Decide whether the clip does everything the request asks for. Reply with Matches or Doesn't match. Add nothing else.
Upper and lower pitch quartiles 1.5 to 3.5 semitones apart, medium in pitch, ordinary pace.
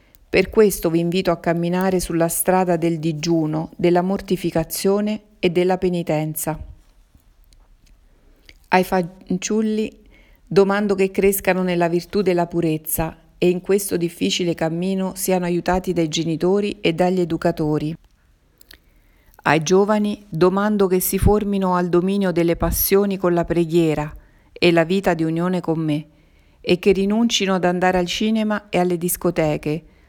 Matches